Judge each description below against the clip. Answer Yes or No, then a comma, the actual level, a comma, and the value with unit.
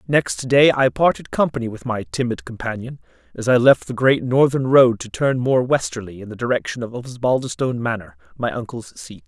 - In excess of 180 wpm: Yes, average, 190 wpm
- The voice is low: Yes, low, 120 Hz